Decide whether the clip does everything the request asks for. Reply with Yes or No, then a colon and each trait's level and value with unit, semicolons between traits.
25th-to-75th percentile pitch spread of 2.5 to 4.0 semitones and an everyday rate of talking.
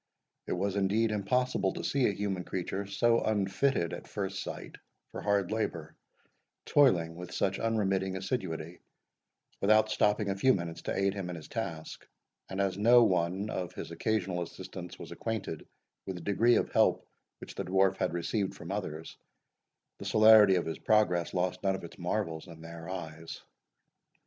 Yes: average, 3.5 semitones; average, 170 wpm